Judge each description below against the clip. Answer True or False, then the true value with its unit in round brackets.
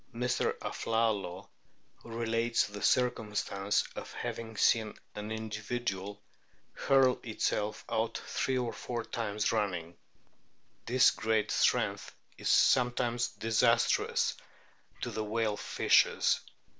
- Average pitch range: False (2.2 semitones)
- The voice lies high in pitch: False (110 Hz)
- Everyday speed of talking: False (105 wpm)